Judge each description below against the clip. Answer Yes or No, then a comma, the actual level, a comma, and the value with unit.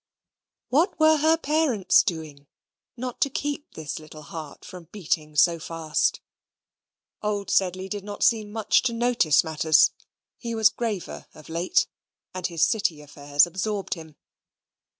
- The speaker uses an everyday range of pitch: No, wide, 6.4 semitones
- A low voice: No, medium, 185 Hz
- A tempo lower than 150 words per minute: Yes, average, 140 wpm